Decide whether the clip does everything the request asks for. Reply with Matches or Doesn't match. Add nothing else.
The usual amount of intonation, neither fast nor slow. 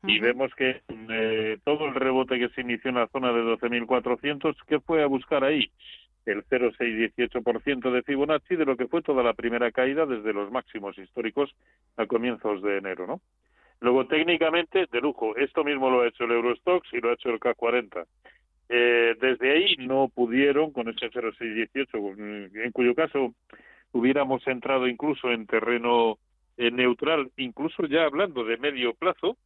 Matches